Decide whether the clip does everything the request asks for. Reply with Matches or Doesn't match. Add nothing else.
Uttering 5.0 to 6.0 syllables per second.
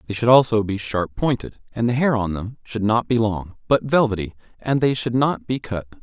Matches